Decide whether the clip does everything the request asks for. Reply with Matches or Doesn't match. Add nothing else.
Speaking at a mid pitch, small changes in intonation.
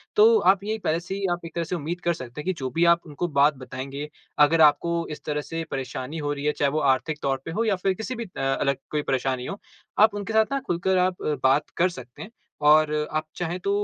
Doesn't match